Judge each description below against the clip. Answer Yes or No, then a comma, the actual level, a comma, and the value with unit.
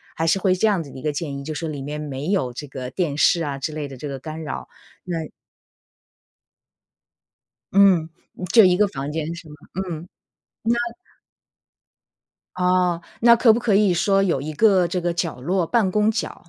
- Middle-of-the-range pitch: Yes, medium, 170 Hz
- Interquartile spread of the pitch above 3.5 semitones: Yes, average, 4.4 semitones